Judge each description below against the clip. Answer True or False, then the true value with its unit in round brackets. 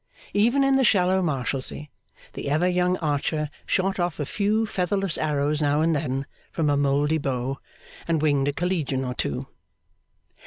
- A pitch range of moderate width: True (4.4 semitones)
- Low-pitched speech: False (155 Hz)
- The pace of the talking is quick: False (160 wpm)